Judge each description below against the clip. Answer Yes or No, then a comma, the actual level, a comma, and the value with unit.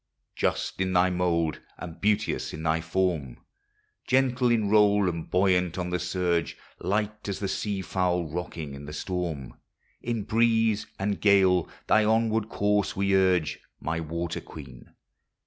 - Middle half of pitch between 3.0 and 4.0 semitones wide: Yes, average, 3.4 semitones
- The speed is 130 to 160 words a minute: Yes, average, 145 wpm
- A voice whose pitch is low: Yes, very low, 95 Hz